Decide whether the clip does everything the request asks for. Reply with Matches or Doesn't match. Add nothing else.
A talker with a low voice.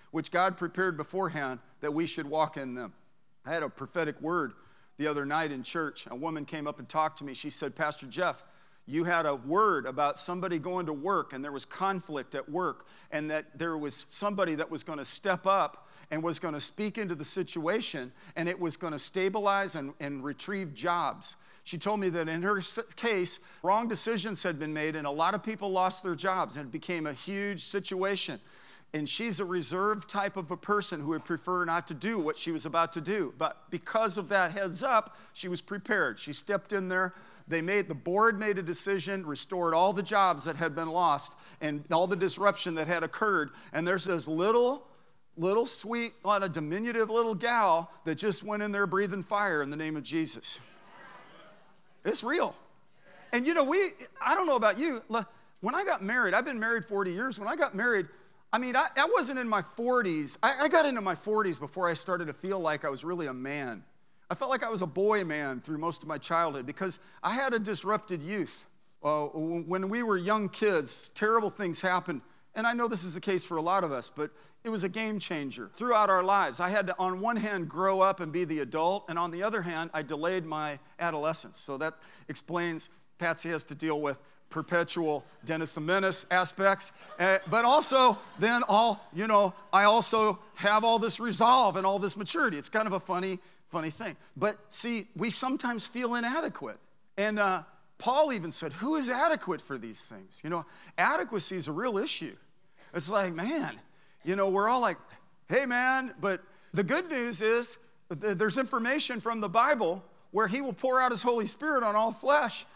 Doesn't match